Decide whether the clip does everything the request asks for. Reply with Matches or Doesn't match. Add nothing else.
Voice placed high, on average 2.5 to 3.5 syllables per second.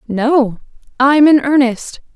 Matches